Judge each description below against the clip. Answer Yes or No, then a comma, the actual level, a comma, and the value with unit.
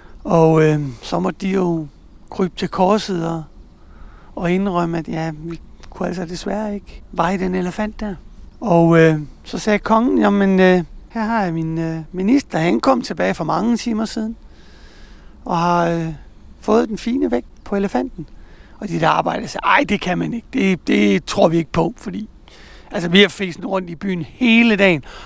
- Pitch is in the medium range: Yes, medium, 180 Hz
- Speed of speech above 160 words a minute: Yes, average, 185 wpm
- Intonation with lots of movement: No, average, 4.1 semitones